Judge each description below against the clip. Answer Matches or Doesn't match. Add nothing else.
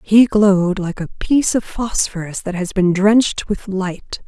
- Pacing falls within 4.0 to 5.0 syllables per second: Matches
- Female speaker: Matches